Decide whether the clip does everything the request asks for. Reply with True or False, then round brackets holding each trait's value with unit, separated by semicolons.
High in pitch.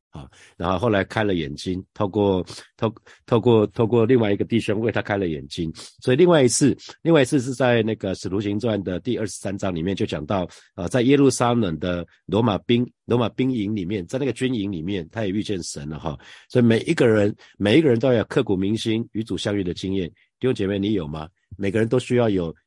False (105 Hz)